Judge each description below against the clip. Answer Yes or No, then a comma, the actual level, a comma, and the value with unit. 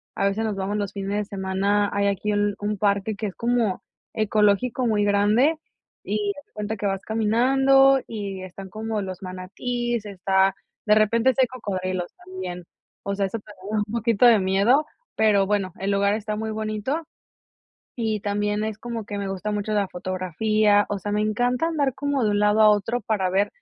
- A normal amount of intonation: No, narrow, 2.0 semitones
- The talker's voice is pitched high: Yes, high, 210 Hz